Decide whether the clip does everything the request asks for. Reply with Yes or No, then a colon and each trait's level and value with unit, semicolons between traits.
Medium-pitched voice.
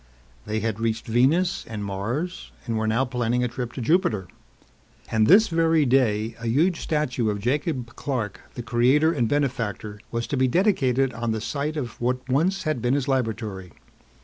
No: low, 125 Hz